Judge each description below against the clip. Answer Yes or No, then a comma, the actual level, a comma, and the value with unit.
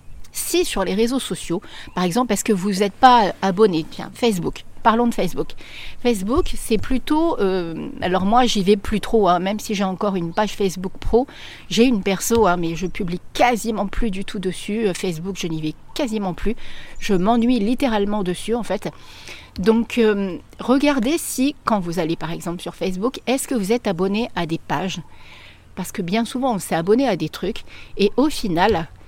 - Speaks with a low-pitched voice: No, high, 205 Hz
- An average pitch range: Yes, average, 4.4 semitones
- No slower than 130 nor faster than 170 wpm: No, average, 190 wpm